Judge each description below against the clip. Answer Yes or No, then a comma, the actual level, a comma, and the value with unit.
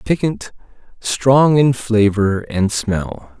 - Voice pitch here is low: Yes, low, 115 Hz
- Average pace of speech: No, slow, 105 wpm